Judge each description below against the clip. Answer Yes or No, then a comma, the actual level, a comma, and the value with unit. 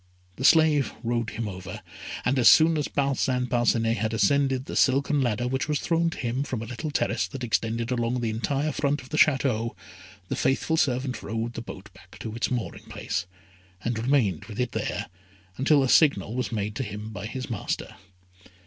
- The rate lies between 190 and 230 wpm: Yes, average, 195 wpm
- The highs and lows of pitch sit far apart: No, average, 3.5 semitones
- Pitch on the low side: Yes, low, 125 Hz